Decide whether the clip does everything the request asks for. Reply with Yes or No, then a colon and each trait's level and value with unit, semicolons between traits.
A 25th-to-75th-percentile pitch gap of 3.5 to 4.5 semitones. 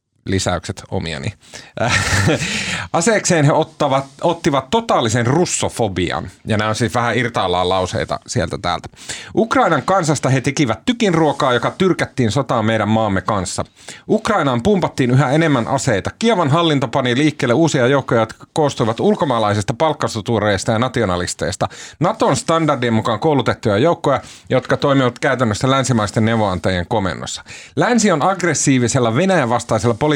No: wide, 5.5 semitones